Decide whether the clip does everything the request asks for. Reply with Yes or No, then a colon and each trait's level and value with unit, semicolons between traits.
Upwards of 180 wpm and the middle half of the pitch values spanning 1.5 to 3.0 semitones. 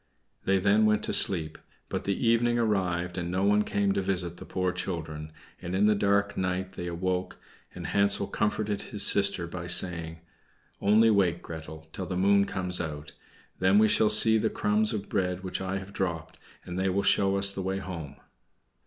Yes: average, 190 wpm; narrow, 2.4 semitones